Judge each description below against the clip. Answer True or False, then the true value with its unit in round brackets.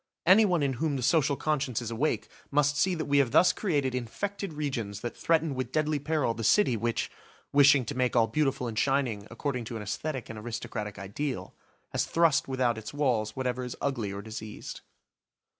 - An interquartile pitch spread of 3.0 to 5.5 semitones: True (4.4 semitones)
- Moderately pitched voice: False (130 Hz)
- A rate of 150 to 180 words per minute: False (190 wpm)